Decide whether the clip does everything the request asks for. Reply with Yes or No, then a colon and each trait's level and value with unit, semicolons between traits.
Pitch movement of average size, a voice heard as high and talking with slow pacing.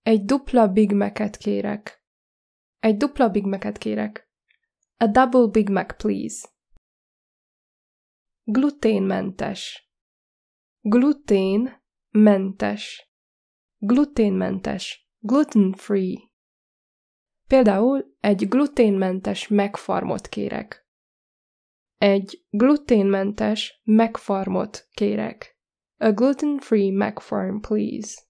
Yes: average, 4.2 semitones; high, 215 Hz; slow, 70 wpm